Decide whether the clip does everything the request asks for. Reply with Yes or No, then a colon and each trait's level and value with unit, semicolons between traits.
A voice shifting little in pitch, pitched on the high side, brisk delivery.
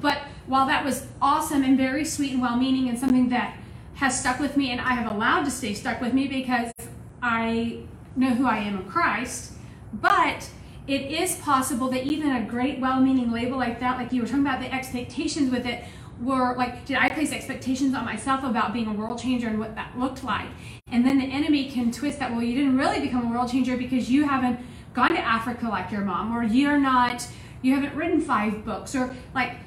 Yes: narrow, 2.1 semitones; very high, 255 Hz; fast, 215 wpm